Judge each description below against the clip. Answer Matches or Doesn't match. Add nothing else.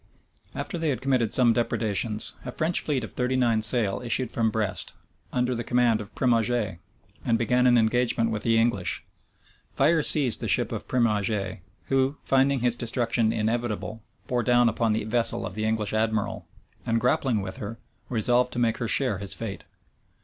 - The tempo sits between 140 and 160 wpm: Doesn't match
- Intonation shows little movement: Matches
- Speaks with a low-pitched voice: Matches